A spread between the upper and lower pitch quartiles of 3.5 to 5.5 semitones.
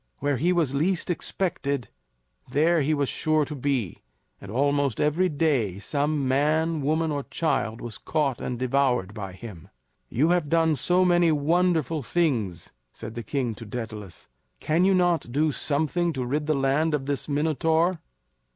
Yes: average, 4.2 semitones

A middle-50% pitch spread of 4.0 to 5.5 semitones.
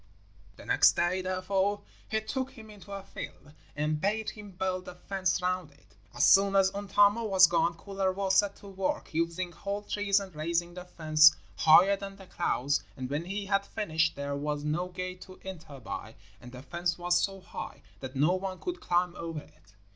No: average, 3.4 semitones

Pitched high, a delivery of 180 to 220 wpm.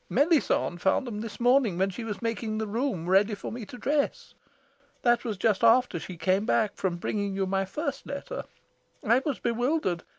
Yes: high, 220 Hz; average, 190 wpm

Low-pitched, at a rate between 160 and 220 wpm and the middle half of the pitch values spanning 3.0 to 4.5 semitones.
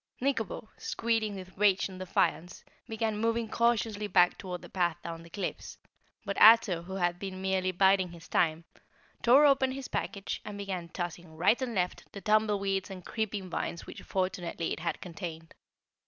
No: high, 190 Hz; average, 170 wpm; average, 3.6 semitones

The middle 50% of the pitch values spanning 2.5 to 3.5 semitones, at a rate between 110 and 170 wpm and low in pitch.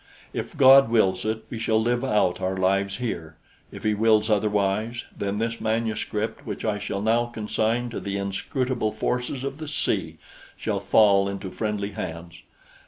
Yes: average, 2.9 semitones; average, 165 wpm; low, 110 Hz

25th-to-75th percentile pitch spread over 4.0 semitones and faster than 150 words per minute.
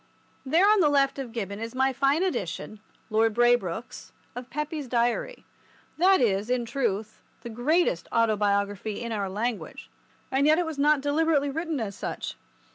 Yes: average, 5.2 semitones; average, 160 wpm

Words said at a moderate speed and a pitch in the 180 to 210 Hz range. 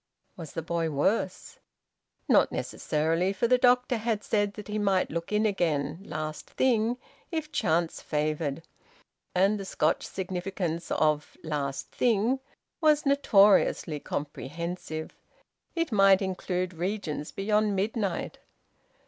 No: slow, 120 wpm; high, 190 Hz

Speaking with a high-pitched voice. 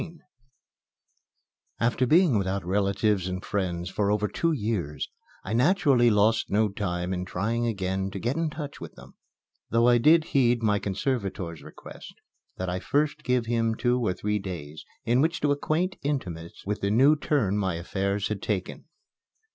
No: low, 105 Hz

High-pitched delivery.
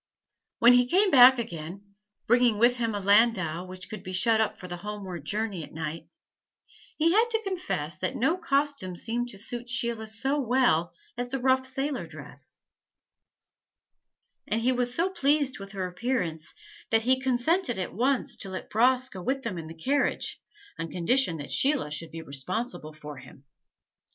Yes: high, 230 Hz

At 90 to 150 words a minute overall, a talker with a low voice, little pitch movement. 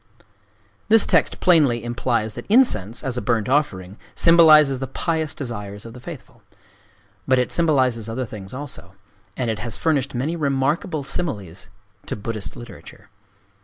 No: average, 145 wpm; low, 125 Hz; wide, 5.4 semitones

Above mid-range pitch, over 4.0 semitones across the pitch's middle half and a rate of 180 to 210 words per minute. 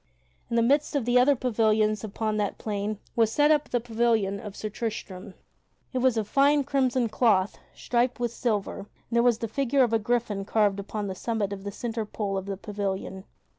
No: high, 220 Hz; average, 3.1 semitones; average, 200 wpm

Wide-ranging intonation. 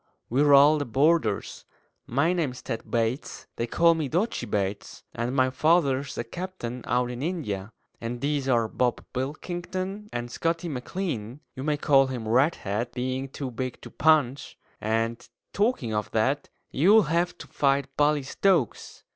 No: average, 5.0 semitones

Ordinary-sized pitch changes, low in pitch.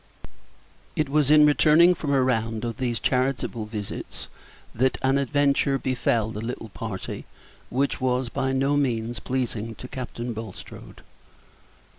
Yes: average, 3.4 semitones; low, 125 Hz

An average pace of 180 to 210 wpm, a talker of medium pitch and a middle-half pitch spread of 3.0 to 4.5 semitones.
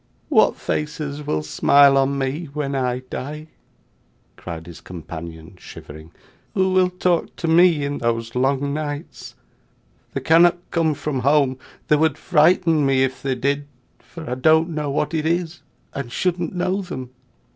No: average, 155 wpm; medium, 145 Hz; average, 3.9 semitones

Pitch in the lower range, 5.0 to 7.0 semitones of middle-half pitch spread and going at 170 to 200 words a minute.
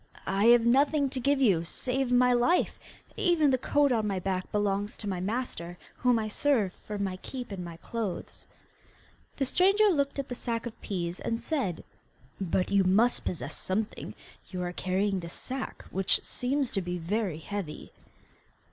No: high, 215 Hz; wide, 5.5 semitones; average, 175 wpm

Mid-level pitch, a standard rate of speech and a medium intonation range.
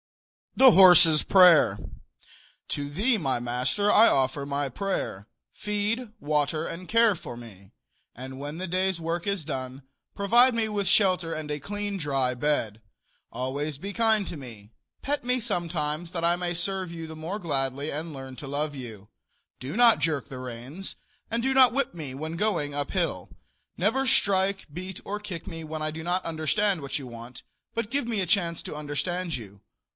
No: medium, 165 Hz; average, 180 wpm; wide, 6.1 semitones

